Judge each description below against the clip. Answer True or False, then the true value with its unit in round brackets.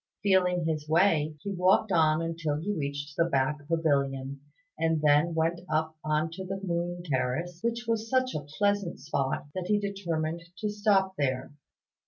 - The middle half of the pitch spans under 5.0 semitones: True (4.0 semitones)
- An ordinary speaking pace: True (165 wpm)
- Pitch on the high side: False (165 Hz)